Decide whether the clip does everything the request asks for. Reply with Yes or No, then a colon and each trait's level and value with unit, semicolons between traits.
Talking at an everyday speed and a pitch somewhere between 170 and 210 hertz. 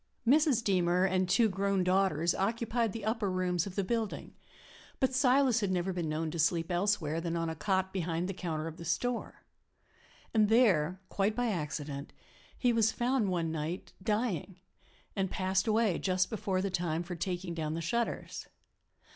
Yes: average, 170 wpm; medium, 185 Hz